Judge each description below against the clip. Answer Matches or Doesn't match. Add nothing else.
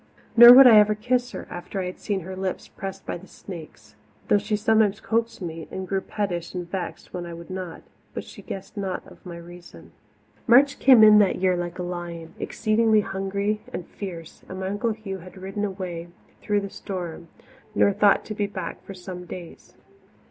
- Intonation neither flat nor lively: Matches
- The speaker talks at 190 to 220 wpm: Matches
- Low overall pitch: Doesn't match